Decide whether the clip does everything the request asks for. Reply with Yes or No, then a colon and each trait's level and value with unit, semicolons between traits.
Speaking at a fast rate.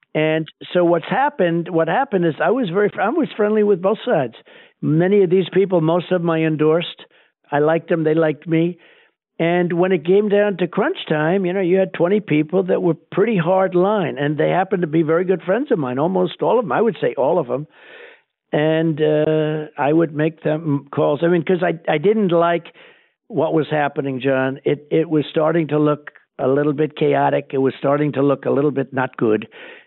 Yes: fast, 215 wpm